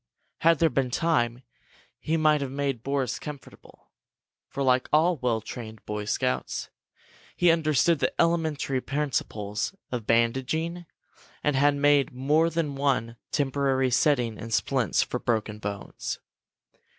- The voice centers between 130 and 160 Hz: Yes, low, 135 Hz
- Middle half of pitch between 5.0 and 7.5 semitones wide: No, average, 4.4 semitones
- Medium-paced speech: No, slow, 130 wpm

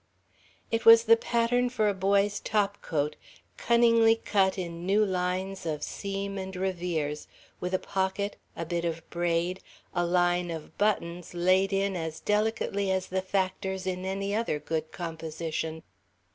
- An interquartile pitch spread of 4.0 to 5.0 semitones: No, average, 2.8 semitones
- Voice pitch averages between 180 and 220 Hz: Yes, high, 190 Hz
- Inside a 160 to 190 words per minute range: No, average, 145 wpm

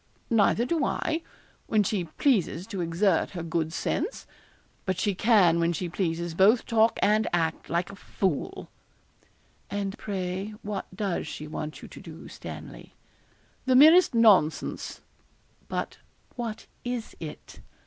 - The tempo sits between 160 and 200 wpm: No, average, 140 wpm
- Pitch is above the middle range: Yes, high, 195 Hz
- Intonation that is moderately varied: Yes, average, 4.7 semitones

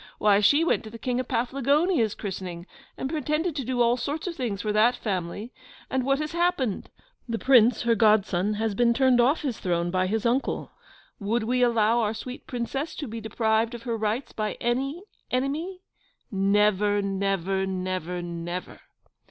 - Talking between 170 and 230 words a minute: Yes, average, 175 wpm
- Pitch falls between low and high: No, high, 230 Hz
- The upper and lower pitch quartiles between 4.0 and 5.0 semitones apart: Yes, average, 4.4 semitones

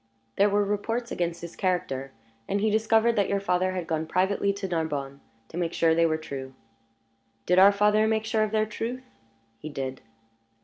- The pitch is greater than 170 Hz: Yes, high, 190 Hz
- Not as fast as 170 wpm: No, average, 185 wpm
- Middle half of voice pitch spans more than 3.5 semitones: Yes, average, 4.6 semitones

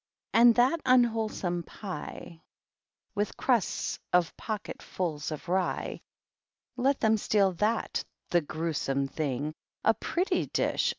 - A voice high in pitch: Yes, high, 200 Hz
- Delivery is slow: Yes, slow, 125 wpm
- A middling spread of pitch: No, wide, 5.7 semitones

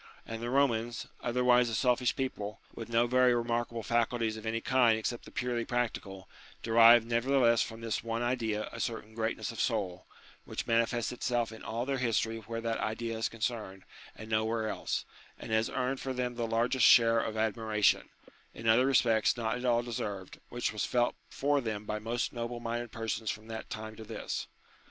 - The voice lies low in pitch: Yes, low, 115 Hz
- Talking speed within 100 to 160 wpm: No, average, 190 wpm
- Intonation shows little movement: Yes, narrow, 1.5 semitones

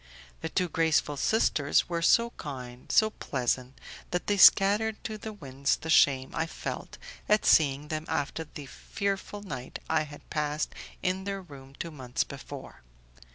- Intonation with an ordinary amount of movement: No, wide, 5.9 semitones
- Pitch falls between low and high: Yes, medium, 155 Hz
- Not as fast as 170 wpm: Yes, average, 155 wpm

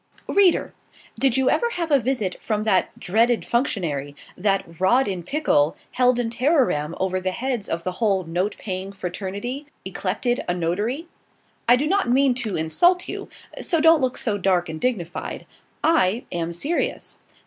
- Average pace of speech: Yes, average, 160 wpm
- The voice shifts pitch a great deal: Yes, wide, 6.3 semitones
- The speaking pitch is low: No, high, 215 Hz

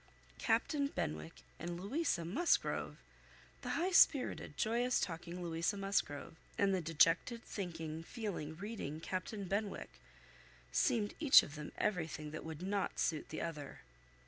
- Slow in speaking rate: Yes, slow, 130 wpm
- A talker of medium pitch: Yes, medium, 180 Hz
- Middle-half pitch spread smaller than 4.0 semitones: No, average, 5.1 semitones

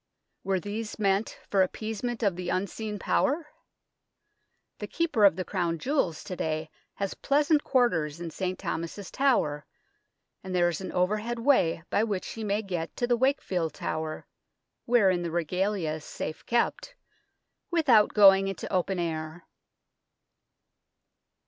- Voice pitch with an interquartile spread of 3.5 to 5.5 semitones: Yes, average, 4.9 semitones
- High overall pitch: Yes, high, 195 Hz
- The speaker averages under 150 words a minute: Yes, average, 140 wpm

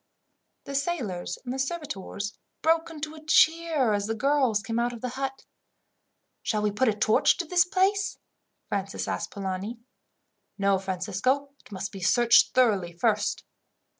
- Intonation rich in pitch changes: Yes, wide, 6.4 semitones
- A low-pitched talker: No, high, 240 Hz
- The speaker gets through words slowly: No, average, 150 wpm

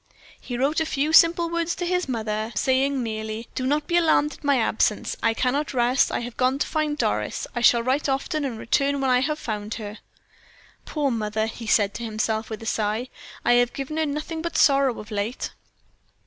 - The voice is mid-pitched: No, very high, 255 Hz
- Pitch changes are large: No, average, 4.8 semitones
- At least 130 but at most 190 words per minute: No, fast, 205 wpm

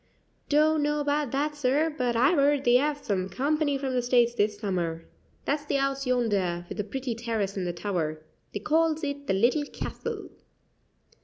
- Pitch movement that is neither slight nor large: No, wide, 6.0 semitones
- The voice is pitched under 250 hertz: No, very high, 255 Hz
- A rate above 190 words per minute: No, average, 180 wpm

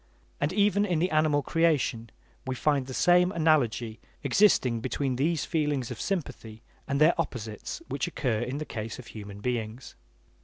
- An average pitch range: No, wide, 5.7 semitones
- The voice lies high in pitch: No, medium, 140 Hz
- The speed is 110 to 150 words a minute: No, average, 160 wpm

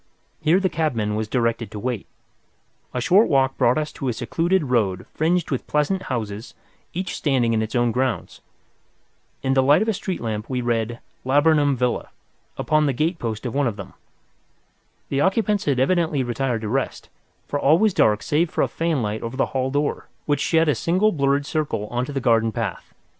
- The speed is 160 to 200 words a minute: Yes, average, 195 wpm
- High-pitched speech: No, low, 135 Hz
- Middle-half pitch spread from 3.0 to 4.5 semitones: No, average, 5.1 semitones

